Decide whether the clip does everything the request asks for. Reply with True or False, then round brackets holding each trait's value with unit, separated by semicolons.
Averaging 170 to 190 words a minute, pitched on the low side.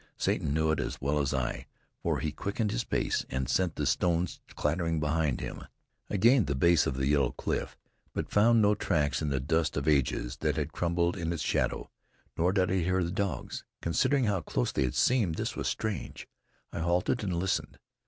False (200 wpm; 80 Hz)